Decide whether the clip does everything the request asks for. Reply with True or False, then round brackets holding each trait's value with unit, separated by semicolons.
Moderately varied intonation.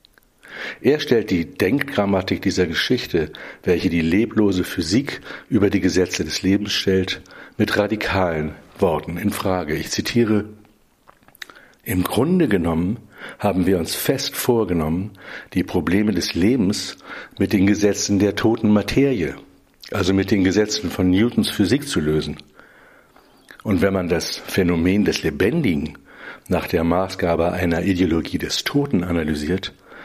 True (3.0 semitones)